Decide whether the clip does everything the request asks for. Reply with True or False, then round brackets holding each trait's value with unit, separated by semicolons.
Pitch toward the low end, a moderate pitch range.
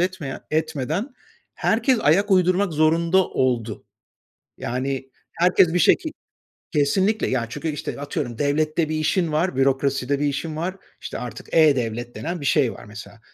False (155 Hz; 4.7 semitones)